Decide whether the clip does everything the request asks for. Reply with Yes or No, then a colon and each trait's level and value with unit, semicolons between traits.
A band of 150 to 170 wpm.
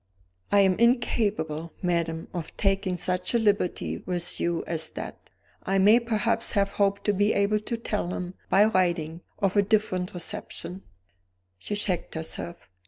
Yes: average, 160 wpm